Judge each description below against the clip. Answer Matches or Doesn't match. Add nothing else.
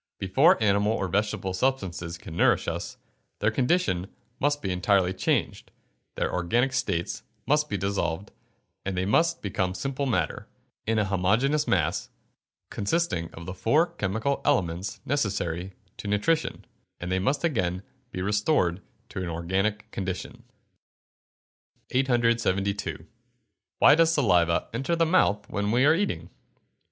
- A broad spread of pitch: Matches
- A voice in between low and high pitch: Doesn't match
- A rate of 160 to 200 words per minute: Doesn't match